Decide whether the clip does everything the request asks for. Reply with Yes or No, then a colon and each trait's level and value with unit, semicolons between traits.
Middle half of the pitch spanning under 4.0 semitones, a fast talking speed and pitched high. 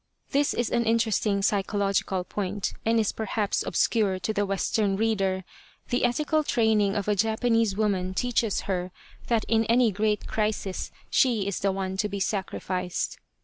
No: narrow, 2.5 semitones; average, 155 wpm; high, 210 Hz